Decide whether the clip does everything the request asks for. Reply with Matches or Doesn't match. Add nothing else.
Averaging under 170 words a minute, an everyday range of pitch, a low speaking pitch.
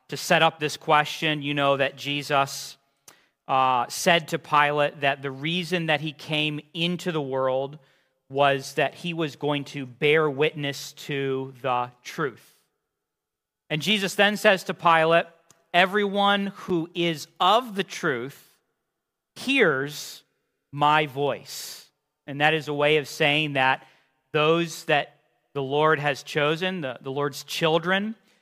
Doesn't match